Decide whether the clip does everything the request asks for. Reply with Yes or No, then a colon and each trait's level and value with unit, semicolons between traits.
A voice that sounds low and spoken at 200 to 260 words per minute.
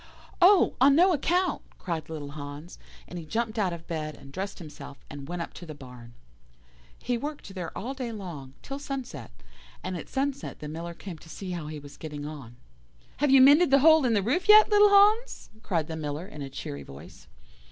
No: medium, 180 Hz; fast, 205 wpm